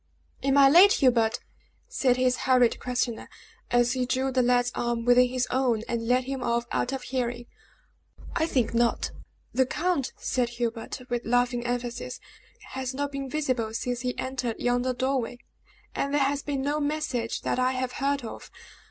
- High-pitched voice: Yes, very high, 250 Hz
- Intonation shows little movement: Yes, narrow, 1.8 semitones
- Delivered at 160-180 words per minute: Yes, average, 170 wpm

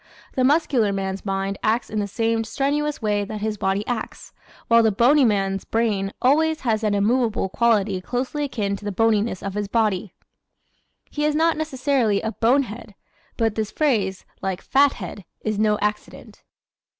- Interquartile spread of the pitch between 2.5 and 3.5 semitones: No, average, 4.0 semitones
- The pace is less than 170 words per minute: Yes, average, 160 wpm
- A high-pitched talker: Yes, high, 220 Hz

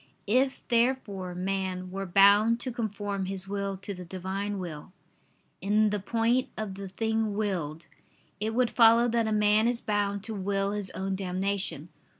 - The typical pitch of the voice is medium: No, high, 200 Hz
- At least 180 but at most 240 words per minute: No, average, 160 wpm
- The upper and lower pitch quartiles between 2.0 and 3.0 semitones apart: Yes, narrow, 2.5 semitones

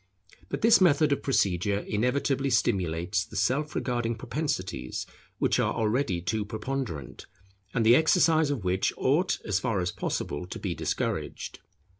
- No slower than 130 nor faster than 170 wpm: Yes, average, 145 wpm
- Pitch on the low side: Yes, low, 115 Hz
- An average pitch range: No, wide, 6.7 semitones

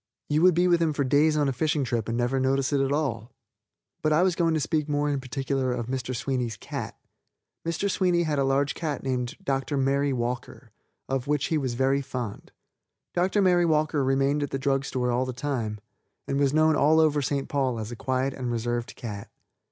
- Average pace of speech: No, fast, 215 wpm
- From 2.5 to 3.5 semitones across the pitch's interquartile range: Yes, average, 3.1 semitones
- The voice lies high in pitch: No, low, 135 Hz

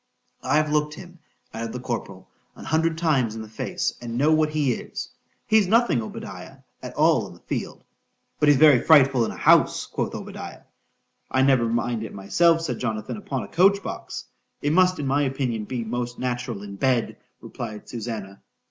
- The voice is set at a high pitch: No, low, 130 Hz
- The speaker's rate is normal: Yes, average, 165 wpm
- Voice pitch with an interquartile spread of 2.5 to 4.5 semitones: No, average, 5.1 semitones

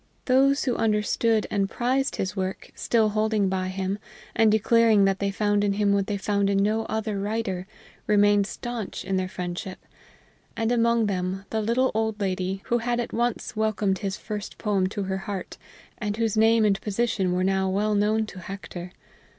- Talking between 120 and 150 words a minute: No, average, 185 wpm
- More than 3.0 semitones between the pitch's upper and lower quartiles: No, narrow, 2.4 semitones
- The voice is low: No, high, 205 Hz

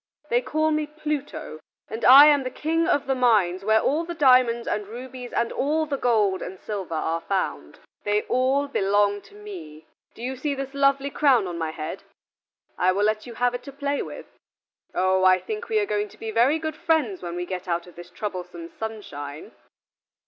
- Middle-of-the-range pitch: No, high, 230 Hz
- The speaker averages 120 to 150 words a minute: No, average, 200 wpm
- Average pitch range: No, wide, 6.8 semitones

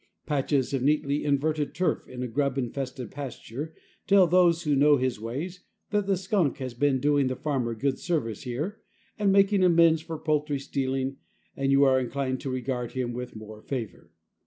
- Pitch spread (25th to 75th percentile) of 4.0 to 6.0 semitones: No, average, 3.6 semitones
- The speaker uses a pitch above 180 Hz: No, medium, 140 Hz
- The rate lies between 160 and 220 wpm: Yes, average, 180 wpm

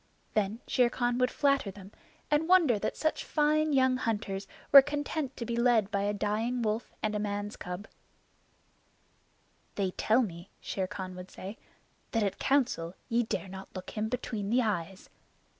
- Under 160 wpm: No, average, 170 wpm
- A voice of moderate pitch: No, high, 220 Hz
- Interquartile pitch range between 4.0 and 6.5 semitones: Yes, average, 4.3 semitones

